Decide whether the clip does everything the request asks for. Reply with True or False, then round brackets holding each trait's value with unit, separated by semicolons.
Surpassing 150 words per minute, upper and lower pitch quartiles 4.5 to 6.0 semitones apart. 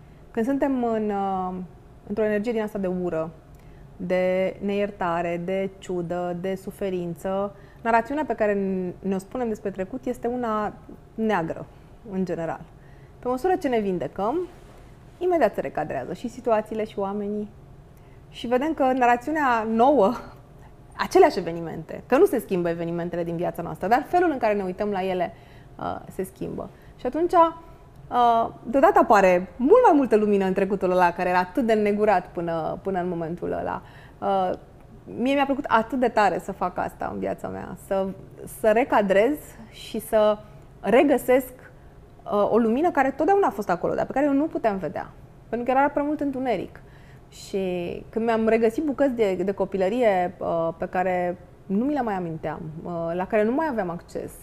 True (160 wpm; 5.4 semitones)